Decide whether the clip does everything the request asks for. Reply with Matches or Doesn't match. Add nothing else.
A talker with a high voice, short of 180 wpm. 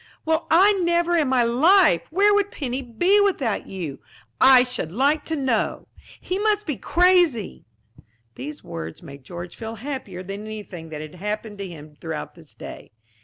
Matches